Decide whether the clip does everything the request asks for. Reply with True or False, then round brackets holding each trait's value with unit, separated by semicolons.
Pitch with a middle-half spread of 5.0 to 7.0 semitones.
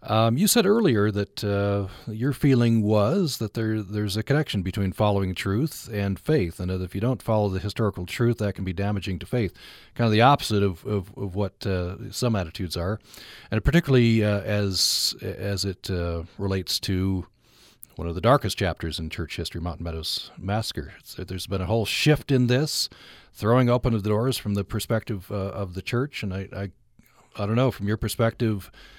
False (3.3 semitones)